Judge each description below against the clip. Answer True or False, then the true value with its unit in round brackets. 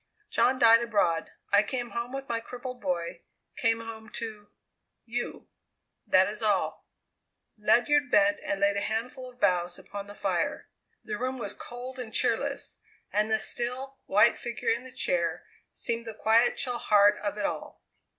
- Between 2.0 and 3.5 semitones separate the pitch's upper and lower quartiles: True (3.2 semitones)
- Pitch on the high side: True (230 Hz)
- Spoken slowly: False (165 wpm)